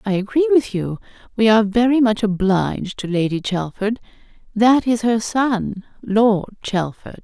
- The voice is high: Yes, high, 215 Hz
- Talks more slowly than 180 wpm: Yes, slow, 135 wpm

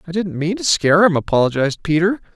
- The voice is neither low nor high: Yes, medium, 170 Hz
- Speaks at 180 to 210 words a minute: Yes, fast, 205 wpm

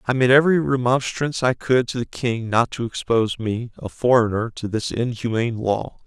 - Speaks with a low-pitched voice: Yes, low, 120 Hz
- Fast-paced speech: No, average, 190 wpm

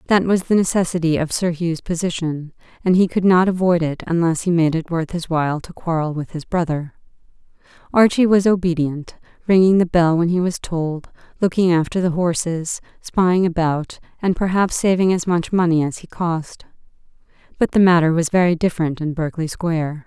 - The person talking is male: No, female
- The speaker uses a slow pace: No, average, 180 wpm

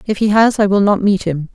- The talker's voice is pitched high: Yes, high, 200 Hz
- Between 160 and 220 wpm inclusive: No, fast, 310 wpm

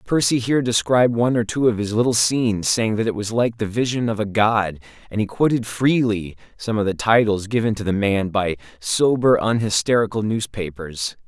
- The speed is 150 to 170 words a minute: No, average, 190 wpm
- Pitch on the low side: Yes, low, 110 Hz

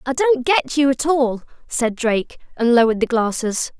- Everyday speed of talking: Yes, average, 190 wpm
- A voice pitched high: Yes, very high, 255 Hz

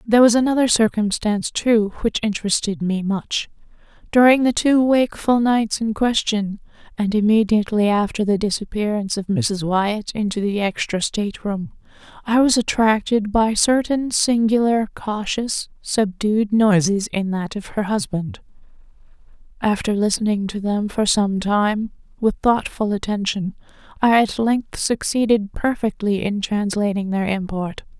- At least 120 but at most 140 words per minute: Yes, slow, 135 wpm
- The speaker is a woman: Yes, female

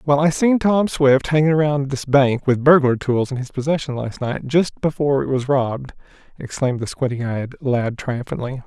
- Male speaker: Yes, male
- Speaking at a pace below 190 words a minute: No, average, 195 wpm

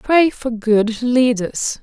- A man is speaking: No, female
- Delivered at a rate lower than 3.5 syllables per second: Yes, 2.9 syllables/s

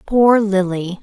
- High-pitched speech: Yes, high, 200 Hz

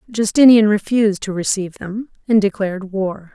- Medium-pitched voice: No, high, 205 Hz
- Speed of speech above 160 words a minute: No, average, 145 wpm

